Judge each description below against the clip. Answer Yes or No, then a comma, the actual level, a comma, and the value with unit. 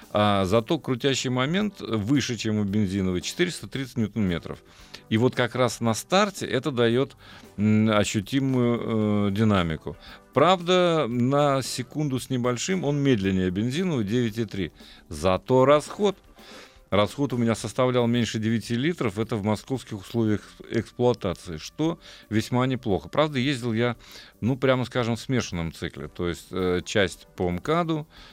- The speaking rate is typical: Yes, average, 135 wpm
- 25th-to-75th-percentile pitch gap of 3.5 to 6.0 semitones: Yes, average, 4.4 semitones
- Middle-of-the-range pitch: No, low, 115 Hz